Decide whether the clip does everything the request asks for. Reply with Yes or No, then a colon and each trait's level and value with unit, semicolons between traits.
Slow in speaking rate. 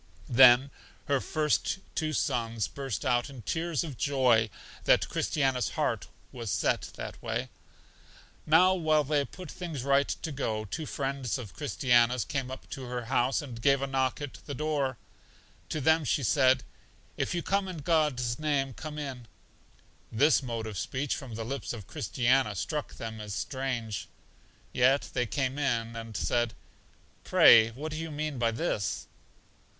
No: average, 165 wpm